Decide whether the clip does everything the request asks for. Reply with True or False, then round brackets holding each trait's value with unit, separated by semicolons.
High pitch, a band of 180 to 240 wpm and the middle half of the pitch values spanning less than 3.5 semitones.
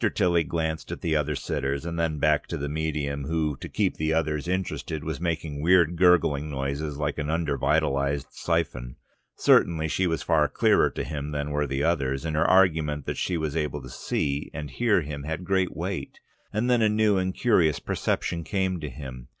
False (80 Hz; 195 wpm; 2.8 semitones)